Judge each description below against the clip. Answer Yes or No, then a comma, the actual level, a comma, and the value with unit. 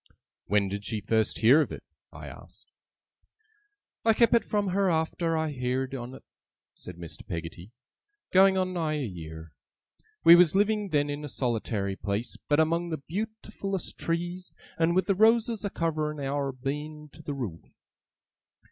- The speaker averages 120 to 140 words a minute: No, average, 165 wpm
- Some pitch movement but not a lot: No, wide, 7.2 semitones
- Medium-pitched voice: Yes, medium, 150 Hz